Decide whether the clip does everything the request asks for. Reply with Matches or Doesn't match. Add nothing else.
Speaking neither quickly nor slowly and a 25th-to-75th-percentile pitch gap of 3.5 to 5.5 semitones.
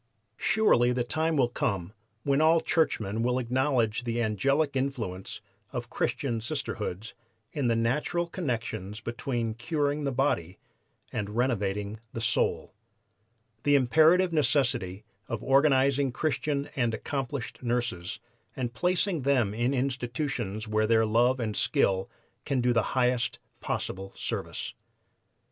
Doesn't match